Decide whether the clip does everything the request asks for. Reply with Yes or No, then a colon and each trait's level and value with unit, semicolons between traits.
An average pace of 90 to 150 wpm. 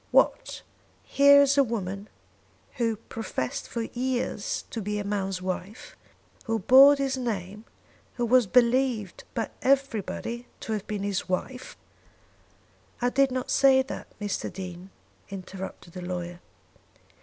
Yes: slow, 135 wpm